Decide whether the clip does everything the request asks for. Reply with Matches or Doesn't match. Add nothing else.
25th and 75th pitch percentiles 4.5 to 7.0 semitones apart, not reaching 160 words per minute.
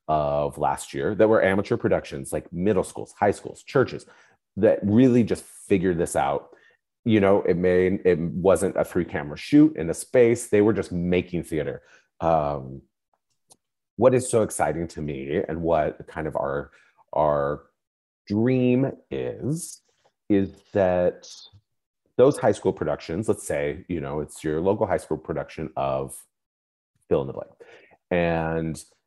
Matches